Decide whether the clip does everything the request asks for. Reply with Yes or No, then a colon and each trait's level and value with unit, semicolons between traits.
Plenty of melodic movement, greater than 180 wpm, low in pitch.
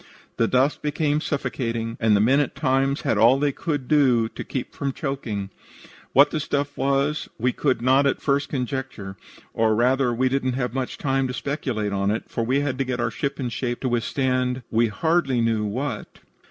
No: average, 3.1 semitones; average, 195 wpm; low, 130 Hz